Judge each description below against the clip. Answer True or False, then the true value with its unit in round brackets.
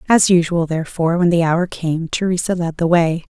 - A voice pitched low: False (170 Hz)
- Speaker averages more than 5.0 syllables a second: True (5.5 syllables/s)